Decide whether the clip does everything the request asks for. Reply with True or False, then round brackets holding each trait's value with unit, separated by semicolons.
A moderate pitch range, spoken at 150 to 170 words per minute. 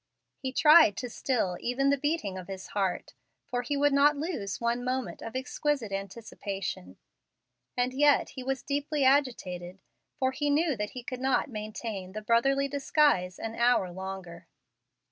False (6.0 semitones; 160 wpm)